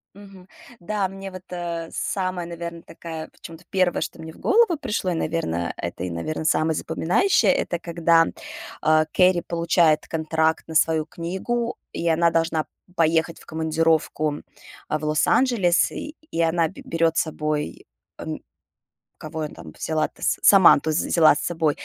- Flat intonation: Yes, narrow, 2.1 semitones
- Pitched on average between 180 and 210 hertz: No, medium, 165 Hz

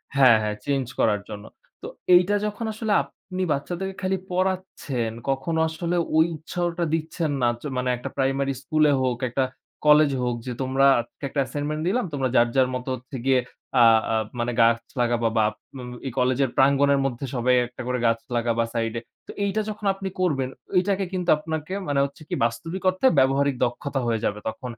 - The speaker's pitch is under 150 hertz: Yes, medium, 140 Hz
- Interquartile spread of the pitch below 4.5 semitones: No, wide, 5.6 semitones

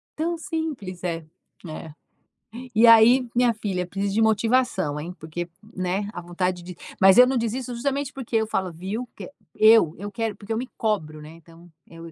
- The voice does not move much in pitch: No, average, 5.2 semitones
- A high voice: Yes, high, 205 Hz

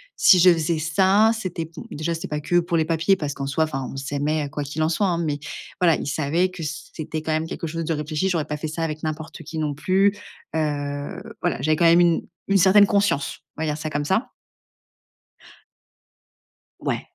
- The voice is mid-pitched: Yes, medium, 160 Hz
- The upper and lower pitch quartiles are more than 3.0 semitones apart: No, narrow, 2.5 semitones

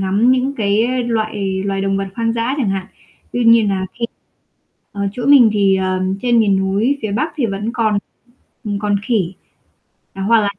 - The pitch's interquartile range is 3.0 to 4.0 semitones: Yes, average, 3.3 semitones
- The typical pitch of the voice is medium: No, high, 215 Hz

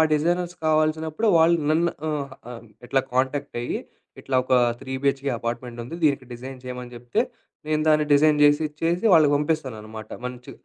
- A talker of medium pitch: Yes, medium, 145 Hz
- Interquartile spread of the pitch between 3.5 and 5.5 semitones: Yes, average, 3.8 semitones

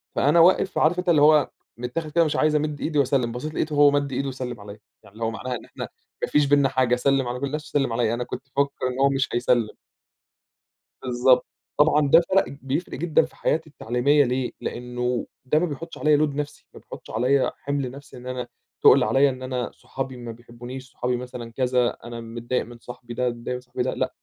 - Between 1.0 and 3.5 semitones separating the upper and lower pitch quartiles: Yes, average, 2.9 semitones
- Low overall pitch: Yes, low, 130 Hz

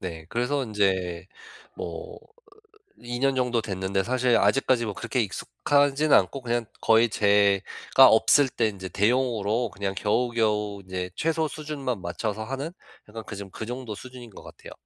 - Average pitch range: Yes, average, 4.2 semitones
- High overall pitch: No, low, 115 Hz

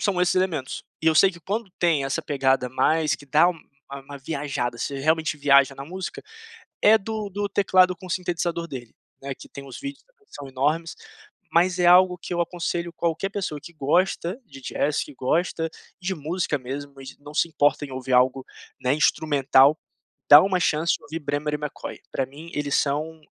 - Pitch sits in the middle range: Yes, medium, 155 Hz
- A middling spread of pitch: Yes, average, 4.2 semitones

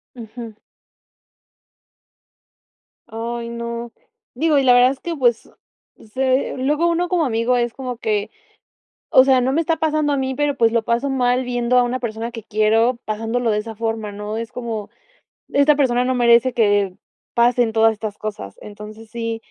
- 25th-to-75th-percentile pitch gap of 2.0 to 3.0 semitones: Yes, narrow, 2.6 semitones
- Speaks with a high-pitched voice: Yes, high, 235 Hz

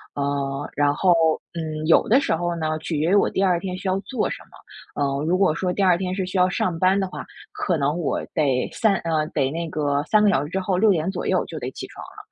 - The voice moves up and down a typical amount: Yes, average, 3.7 semitones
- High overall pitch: No, medium, 170 Hz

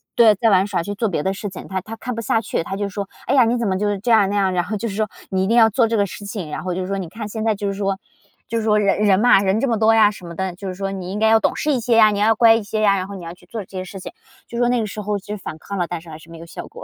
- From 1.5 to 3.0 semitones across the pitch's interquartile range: Yes, average, 2.7 semitones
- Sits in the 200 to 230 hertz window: Yes, high, 205 Hz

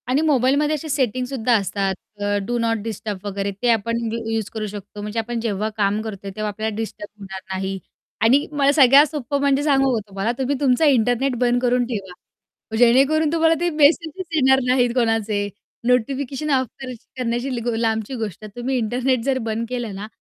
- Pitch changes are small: No, average, 3.9 semitones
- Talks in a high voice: Yes, high, 240 Hz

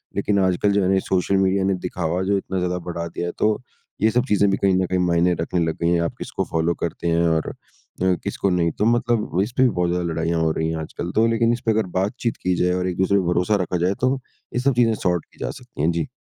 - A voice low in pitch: Yes, very low, 90 Hz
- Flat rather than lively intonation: No, average, 3.3 semitones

